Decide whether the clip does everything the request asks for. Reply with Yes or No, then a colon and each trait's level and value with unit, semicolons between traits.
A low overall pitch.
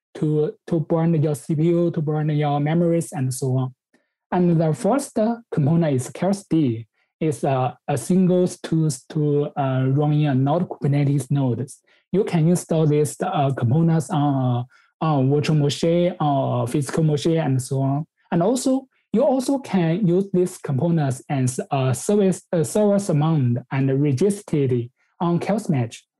No: medium, 155 Hz